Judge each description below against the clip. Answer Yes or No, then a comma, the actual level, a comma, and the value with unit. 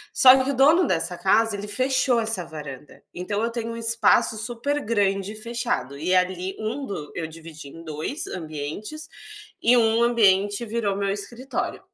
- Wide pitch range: No, average, 4.9 semitones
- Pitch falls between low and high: No, high, 210 Hz